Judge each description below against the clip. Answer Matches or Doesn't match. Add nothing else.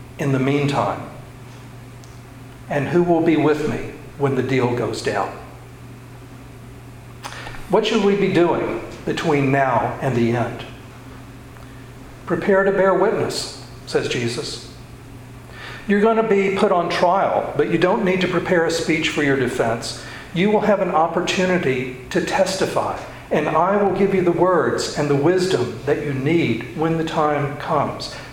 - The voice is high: Doesn't match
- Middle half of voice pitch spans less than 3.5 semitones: Doesn't match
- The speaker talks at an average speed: Matches